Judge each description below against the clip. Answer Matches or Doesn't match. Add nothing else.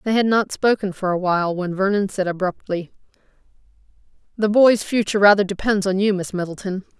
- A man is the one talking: Doesn't match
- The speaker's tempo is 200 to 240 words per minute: Doesn't match